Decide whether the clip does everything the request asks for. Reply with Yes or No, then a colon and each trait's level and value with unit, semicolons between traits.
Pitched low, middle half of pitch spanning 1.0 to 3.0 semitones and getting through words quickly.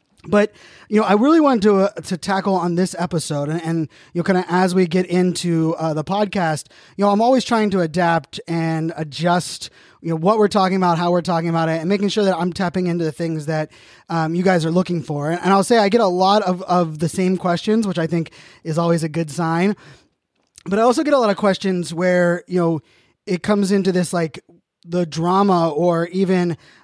No: medium, 180 Hz; average, 2.7 semitones; fast, 230 wpm